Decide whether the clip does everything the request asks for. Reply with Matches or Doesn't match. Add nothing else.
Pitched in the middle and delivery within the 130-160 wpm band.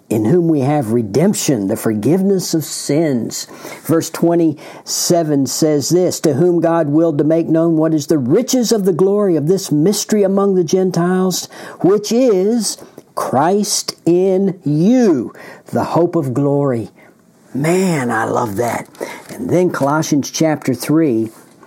Matches